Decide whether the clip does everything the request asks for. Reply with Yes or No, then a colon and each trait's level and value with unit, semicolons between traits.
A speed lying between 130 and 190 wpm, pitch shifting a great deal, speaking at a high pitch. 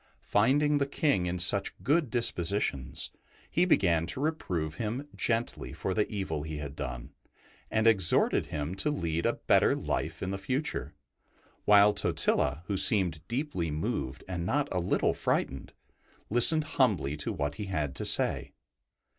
No: average, 155 wpm; wide, 7.4 semitones; very low, 95 Hz